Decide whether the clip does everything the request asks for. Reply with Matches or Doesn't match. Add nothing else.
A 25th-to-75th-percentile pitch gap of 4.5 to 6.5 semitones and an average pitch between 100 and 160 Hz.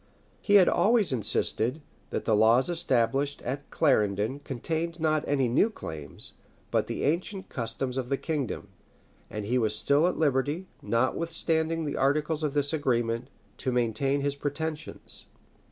Matches